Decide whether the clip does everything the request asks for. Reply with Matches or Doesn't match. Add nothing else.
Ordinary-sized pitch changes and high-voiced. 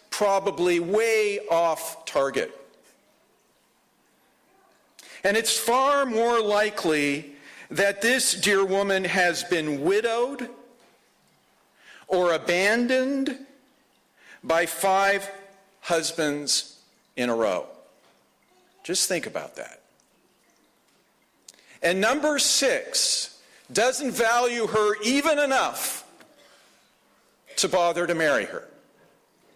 Doesn't match